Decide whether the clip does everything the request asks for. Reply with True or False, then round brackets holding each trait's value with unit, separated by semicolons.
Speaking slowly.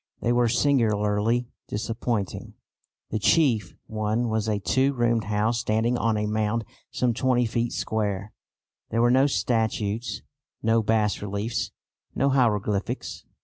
True (130 wpm)